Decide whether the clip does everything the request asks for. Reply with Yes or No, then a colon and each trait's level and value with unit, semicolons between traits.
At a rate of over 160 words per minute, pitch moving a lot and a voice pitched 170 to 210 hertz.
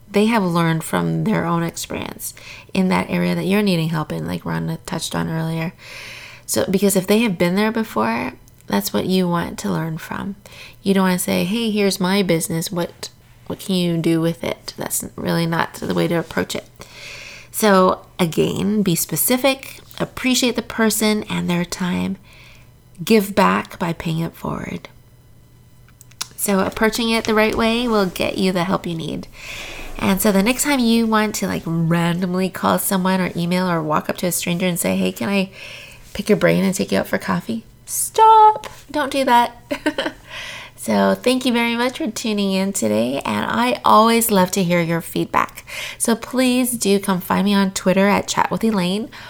No: average, 185 wpm; average, 4.4 semitones; medium, 185 Hz